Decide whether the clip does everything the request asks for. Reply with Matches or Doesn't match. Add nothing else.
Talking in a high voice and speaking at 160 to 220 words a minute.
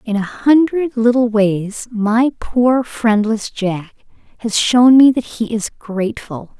Doesn't match